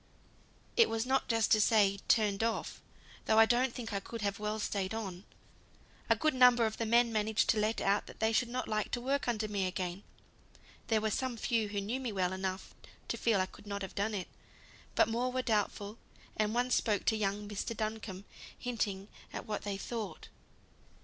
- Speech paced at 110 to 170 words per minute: No, average, 200 wpm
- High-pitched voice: Yes, high, 215 Hz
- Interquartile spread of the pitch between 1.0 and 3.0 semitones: Yes, narrow, 2.6 semitones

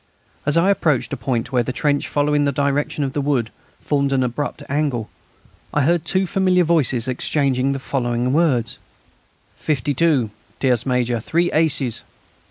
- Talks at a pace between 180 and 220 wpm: No, average, 160 wpm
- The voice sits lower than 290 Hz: Yes, medium, 140 Hz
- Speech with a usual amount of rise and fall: Yes, average, 3.2 semitones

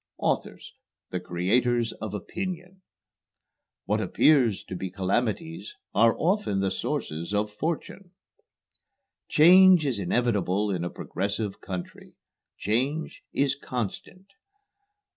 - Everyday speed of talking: No, slow, 105 wpm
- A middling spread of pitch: No, wide, 8.8 semitones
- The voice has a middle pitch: No, low, 115 Hz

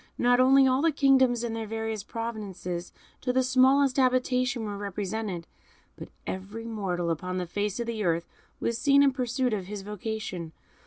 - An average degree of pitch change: Yes, average, 4.4 semitones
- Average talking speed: Yes, average, 170 wpm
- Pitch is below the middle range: No, high, 225 Hz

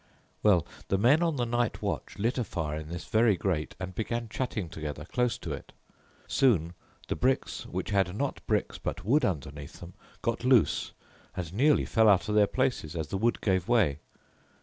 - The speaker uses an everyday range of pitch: No, wide, 5.8 semitones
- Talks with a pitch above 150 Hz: No, low, 100 Hz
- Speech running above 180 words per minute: Yes, average, 190 wpm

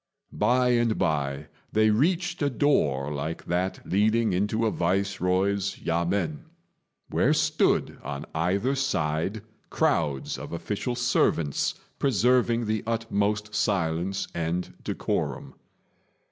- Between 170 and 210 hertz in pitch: No, low, 100 Hz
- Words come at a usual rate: No, slow, 105 wpm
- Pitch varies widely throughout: Yes, wide, 5.7 semitones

